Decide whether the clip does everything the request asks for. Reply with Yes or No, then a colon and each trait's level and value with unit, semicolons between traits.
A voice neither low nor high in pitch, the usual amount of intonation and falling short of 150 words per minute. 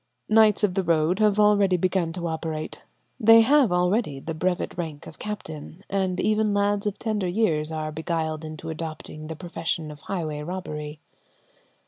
No: medium, 175 Hz; average, 4.5 semitones; average, 160 wpm